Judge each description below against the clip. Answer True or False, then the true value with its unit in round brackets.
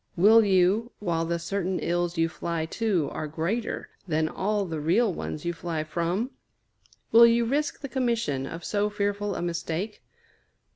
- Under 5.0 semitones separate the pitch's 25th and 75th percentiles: True (4.6 semitones)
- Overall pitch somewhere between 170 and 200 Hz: True (185 Hz)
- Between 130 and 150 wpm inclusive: False (160 wpm)